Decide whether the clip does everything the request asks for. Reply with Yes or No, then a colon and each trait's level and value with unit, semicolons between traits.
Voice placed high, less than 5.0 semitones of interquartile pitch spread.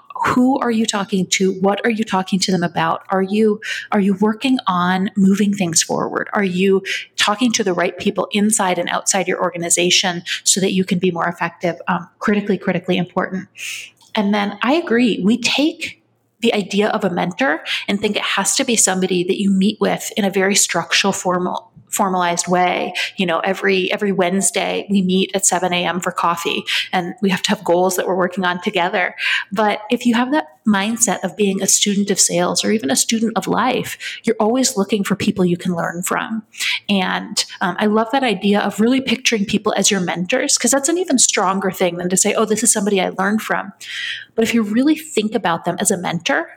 Yes: high, 195 Hz; average, 2.9 semitones